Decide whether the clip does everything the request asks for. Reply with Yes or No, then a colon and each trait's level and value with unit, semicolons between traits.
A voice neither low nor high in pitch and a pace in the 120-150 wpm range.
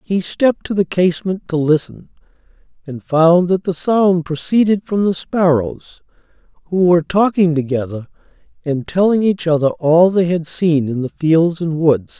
No: medium, 170 Hz; average, 160 wpm